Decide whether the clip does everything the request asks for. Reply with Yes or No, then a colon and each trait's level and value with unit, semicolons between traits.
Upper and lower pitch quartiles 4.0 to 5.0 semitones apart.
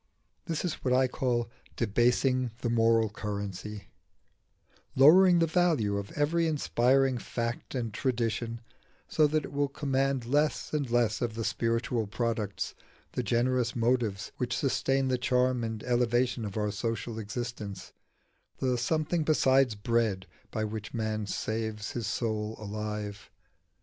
No: average, 3.3 semitones